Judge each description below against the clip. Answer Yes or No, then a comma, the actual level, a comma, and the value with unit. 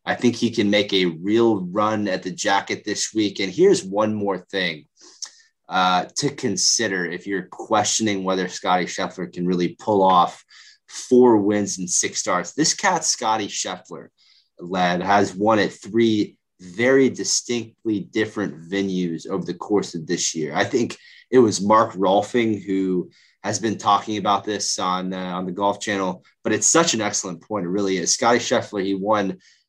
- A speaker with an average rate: Yes, average, 175 wpm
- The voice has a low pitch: Yes, low, 100 Hz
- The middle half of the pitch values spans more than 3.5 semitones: No, average, 2.9 semitones